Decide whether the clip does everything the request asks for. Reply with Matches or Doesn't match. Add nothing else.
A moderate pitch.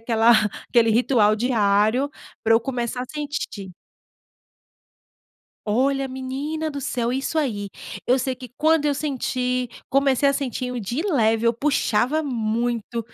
Doesn't match